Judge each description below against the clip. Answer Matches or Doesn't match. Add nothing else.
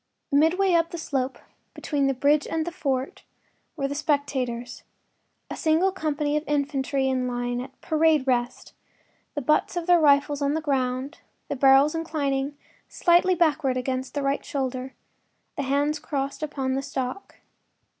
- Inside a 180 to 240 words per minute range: Doesn't match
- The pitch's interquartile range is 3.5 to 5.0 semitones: Doesn't match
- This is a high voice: Matches